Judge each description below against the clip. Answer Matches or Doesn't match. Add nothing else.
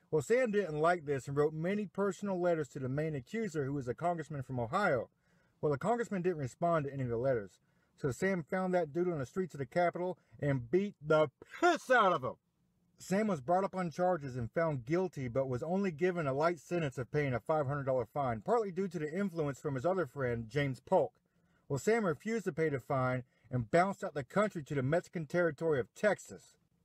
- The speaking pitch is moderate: Matches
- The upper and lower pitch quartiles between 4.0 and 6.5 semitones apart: Matches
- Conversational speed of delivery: Doesn't match